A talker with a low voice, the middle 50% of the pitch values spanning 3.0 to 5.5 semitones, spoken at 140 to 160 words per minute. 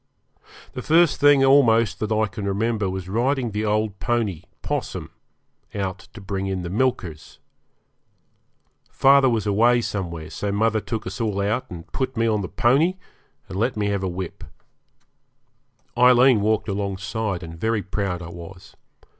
Yes: low, 105 Hz; average, 3.7 semitones; average, 155 wpm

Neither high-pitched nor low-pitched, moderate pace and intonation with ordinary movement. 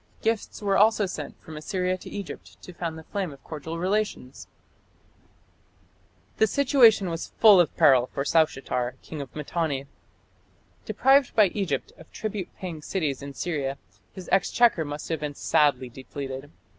No: medium, 165 Hz; average, 150 wpm; wide, 5.8 semitones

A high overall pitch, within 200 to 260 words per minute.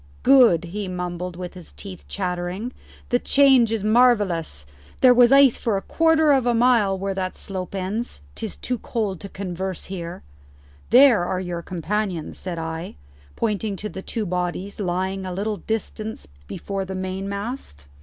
No: high, 195 Hz; average, 160 wpm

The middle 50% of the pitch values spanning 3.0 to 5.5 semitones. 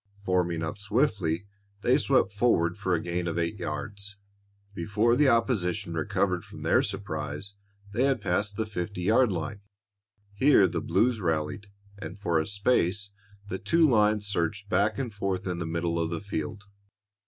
Yes: average, 3.7 semitones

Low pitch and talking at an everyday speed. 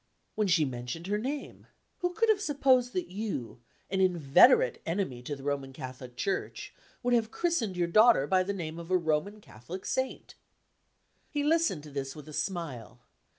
No: medium, 185 Hz; average, 175 wpm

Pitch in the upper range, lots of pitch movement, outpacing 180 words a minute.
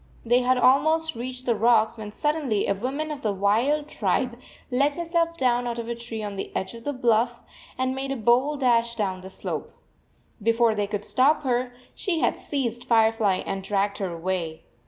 No: high, 235 Hz; average, 3.9 semitones; fast, 205 wpm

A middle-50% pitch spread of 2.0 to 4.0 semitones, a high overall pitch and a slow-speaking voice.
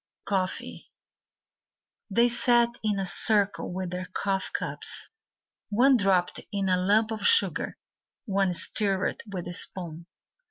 Yes: average, 3.0 semitones; high, 195 Hz; slow, 125 wpm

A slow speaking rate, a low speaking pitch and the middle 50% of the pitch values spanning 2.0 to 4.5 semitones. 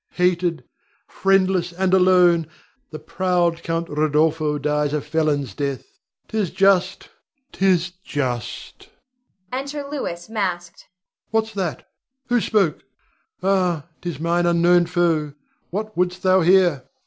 No: slow, 115 wpm; medium, 175 Hz; average, 3.3 semitones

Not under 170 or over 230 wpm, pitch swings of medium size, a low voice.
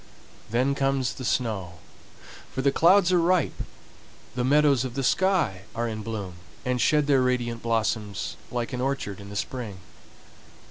No: average, 155 wpm; average, 4.1 semitones; low, 125 Hz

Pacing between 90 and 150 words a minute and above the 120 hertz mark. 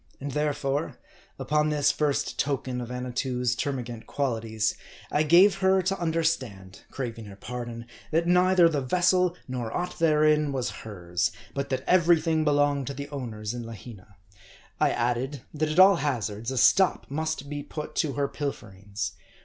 No: average, 160 wpm; medium, 140 Hz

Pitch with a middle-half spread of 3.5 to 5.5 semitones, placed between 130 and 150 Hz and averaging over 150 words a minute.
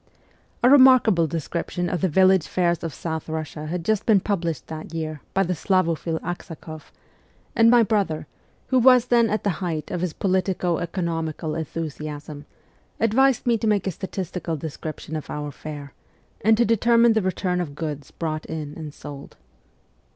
No: average, 4.5 semitones; medium, 170 Hz; average, 165 wpm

